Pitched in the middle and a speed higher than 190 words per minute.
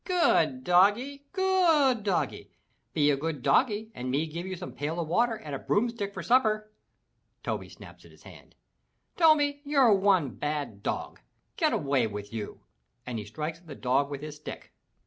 No: medium, 180 Hz; average, 175 wpm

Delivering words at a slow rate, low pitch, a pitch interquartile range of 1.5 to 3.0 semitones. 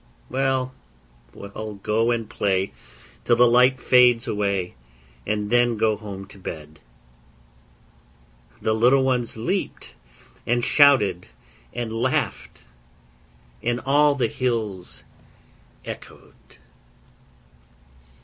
No: slow, 95 wpm; low, 115 Hz; average, 3.6 semitones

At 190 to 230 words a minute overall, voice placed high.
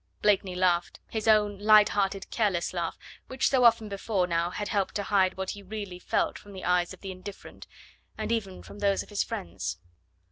Yes: average, 200 wpm; high, 200 Hz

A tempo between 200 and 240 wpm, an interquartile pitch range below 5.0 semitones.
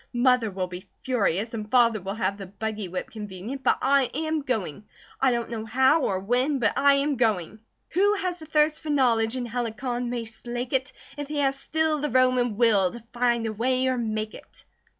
Yes: fast, 205 wpm; average, 3.9 semitones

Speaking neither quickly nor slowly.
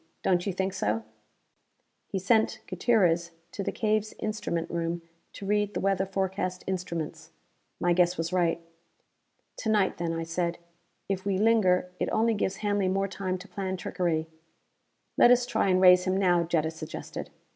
Yes: average, 165 wpm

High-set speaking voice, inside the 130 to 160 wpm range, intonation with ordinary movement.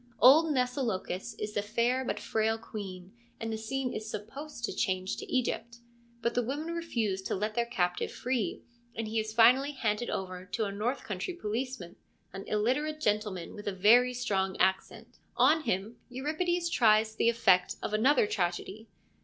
No: high, 225 Hz; average, 170 wpm; average, 3.9 semitones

